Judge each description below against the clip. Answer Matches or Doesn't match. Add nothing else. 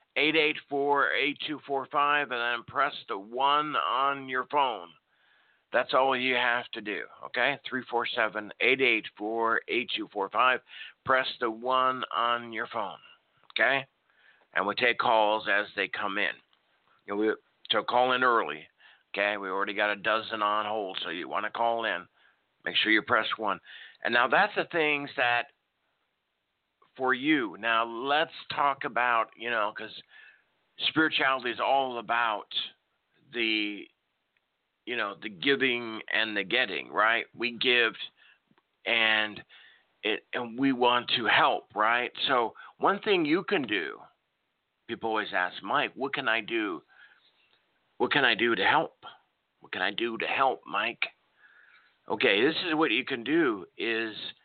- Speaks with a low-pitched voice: Matches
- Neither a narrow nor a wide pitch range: Matches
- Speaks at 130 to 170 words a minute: Matches